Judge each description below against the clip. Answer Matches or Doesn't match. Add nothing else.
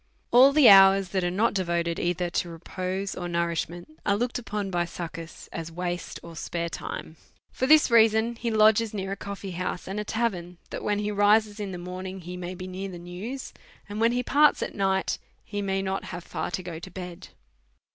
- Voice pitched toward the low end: Doesn't match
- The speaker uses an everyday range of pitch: Matches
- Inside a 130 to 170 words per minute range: Doesn't match